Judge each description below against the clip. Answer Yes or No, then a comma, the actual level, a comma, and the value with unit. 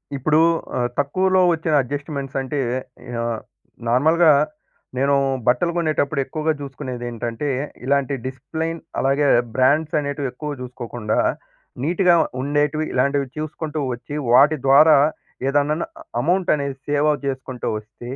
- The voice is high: No, medium, 140 Hz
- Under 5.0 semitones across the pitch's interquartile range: Yes, average, 3.0 semitones